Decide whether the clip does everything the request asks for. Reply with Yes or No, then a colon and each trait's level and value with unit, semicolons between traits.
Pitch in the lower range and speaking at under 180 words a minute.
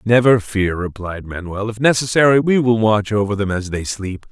No: low, 110 Hz; average, 195 wpm